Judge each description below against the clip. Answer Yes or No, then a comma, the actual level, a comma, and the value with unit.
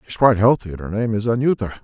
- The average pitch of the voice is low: Yes, low, 110 Hz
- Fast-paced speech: Yes, fast, 295 wpm